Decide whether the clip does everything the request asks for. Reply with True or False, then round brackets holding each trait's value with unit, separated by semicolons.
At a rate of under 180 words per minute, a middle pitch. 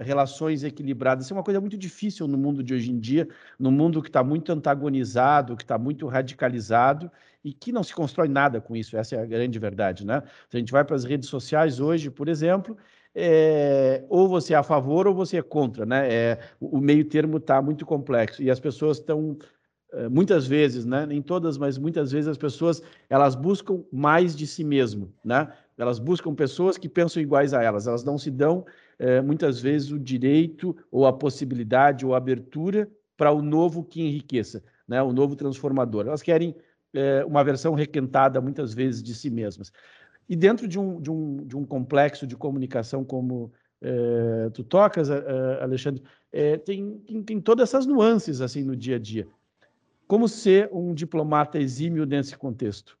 False (185 wpm; 145 Hz)